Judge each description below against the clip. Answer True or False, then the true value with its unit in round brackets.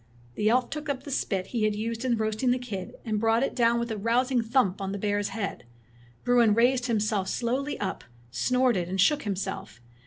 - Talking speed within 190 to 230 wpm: True (205 wpm)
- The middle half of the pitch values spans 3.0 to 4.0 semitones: True (3.4 semitones)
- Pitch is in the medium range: False (230 Hz)